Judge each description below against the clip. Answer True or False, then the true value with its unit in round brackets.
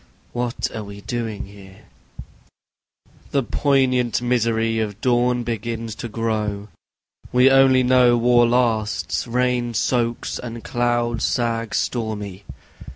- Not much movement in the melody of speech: True (2.0 semitones)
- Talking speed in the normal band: False (110 wpm)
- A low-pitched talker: True (120 Hz)